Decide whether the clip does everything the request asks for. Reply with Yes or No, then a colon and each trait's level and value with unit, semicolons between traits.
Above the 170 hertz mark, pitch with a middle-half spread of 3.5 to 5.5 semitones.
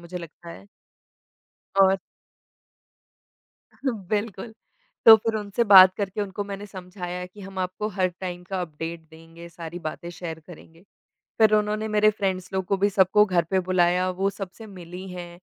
No: medium, 185 Hz; narrow, 2.6 semitones